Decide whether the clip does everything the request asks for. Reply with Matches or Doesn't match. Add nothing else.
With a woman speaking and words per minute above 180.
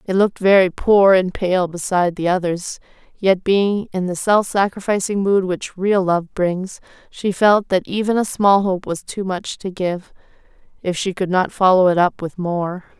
Matches